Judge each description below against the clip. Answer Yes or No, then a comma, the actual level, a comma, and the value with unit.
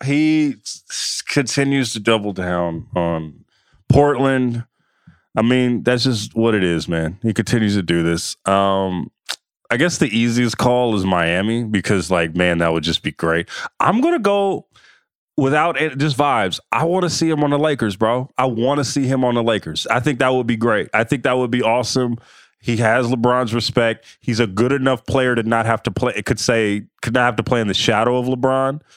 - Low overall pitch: Yes, low, 120 Hz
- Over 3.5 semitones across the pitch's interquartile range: Yes, average, 3.9 semitones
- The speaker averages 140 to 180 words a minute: No, fast, 205 wpm